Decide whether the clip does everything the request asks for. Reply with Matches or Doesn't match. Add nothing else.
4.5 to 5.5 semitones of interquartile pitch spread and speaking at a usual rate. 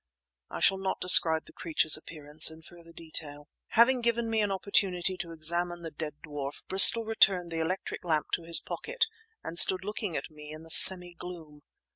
Doesn't match